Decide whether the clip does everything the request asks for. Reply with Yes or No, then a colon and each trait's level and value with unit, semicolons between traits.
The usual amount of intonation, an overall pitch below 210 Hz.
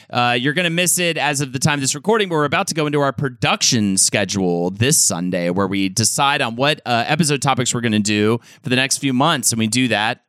Yes: average, 4.9 semitones; low, 135 Hz